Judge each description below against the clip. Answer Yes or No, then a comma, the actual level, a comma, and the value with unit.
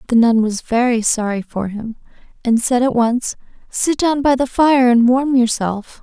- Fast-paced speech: No, average, 190 wpm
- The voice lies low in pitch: No, high, 240 Hz